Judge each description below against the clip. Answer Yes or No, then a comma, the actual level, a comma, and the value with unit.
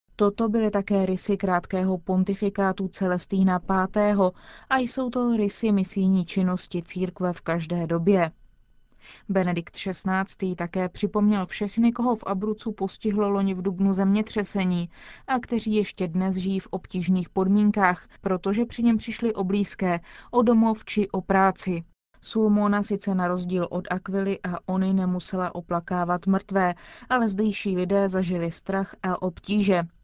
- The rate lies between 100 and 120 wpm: No, average, 135 wpm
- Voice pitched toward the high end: Yes, high, 195 Hz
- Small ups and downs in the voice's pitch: Yes, narrow, 2.2 semitones